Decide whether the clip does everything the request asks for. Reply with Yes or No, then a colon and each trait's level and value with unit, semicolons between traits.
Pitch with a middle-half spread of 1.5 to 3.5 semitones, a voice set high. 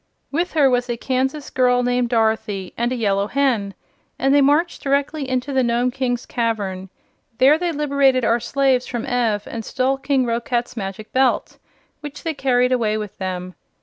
Yes: average, 3.1 semitones; very high, 250 Hz